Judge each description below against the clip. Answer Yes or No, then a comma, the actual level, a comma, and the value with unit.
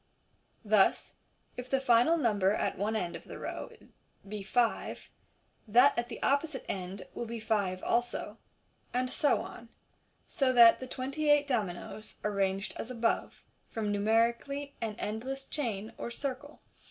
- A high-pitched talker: Yes, high, 235 Hz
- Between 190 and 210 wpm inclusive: No, average, 150 wpm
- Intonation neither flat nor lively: Yes, average, 4.0 semitones